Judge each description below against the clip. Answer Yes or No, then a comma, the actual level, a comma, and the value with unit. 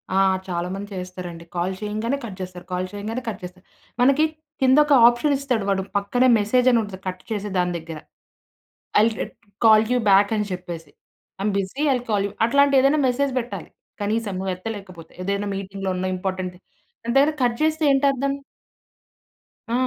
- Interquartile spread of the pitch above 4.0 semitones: Yes, average, 5.1 semitones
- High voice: Yes, high, 205 Hz